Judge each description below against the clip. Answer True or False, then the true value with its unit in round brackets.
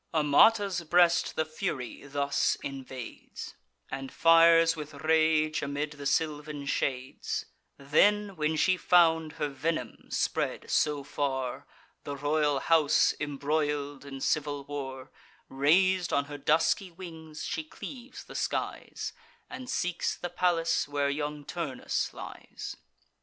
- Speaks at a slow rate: True (120 wpm)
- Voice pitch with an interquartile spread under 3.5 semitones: True (2.7 semitones)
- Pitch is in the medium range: True (150 Hz)